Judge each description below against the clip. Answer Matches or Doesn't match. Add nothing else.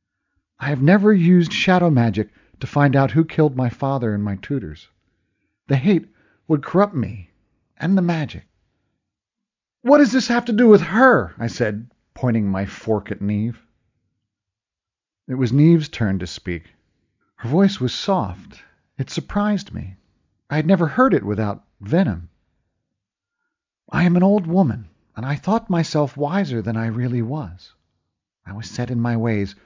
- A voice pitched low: Matches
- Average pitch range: Doesn't match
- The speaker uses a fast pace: Doesn't match